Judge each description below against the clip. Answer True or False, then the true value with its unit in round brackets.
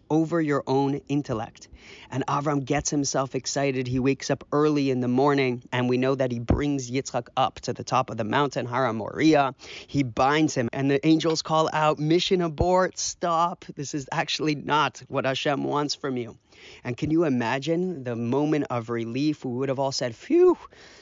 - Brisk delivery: False (190 wpm)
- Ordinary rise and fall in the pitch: True (3.2 semitones)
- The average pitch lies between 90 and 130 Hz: False (140 Hz)